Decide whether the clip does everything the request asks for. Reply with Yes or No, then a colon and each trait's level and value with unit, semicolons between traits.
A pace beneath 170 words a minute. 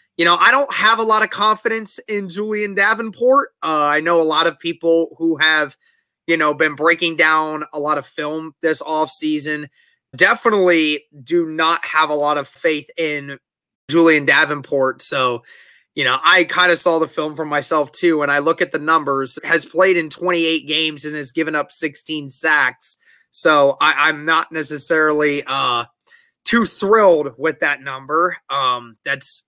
No: average, 175 wpm